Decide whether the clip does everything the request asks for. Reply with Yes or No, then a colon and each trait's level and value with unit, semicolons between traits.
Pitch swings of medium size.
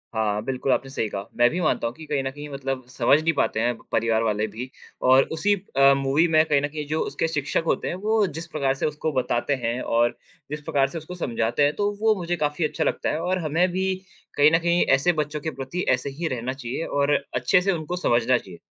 Yes: average, 4.3 semitones